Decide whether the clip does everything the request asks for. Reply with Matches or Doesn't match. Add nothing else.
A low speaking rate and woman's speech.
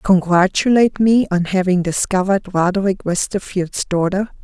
Matches